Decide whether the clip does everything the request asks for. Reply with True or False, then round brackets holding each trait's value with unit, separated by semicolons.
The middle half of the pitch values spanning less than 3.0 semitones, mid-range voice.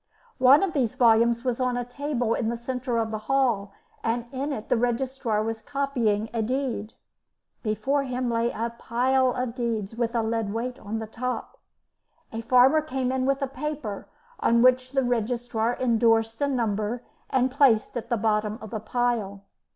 False (2.4 semitones; 240 Hz)